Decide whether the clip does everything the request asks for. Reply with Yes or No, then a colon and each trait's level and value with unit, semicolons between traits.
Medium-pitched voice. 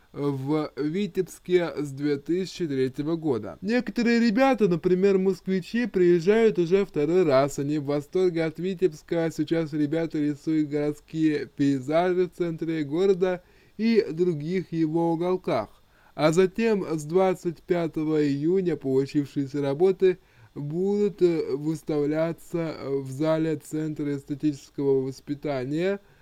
Yes: medium, 165 Hz